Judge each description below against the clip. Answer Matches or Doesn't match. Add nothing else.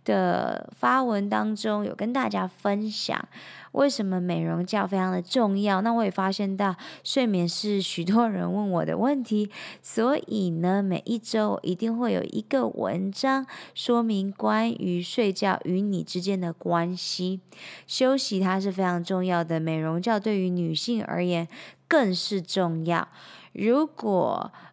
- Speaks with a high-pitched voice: Matches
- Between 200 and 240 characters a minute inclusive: Matches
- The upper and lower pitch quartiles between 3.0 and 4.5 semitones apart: Matches